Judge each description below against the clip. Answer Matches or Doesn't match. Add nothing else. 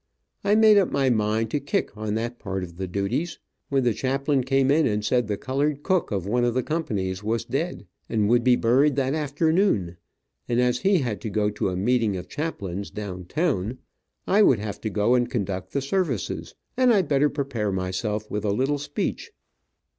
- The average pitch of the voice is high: Doesn't match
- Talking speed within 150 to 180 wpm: Doesn't match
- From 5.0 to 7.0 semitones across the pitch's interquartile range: Matches